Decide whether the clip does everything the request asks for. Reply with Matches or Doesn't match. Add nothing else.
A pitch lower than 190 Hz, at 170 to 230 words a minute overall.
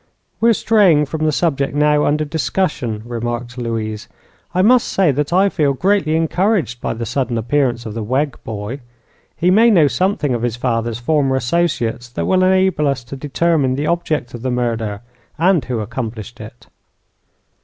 Matches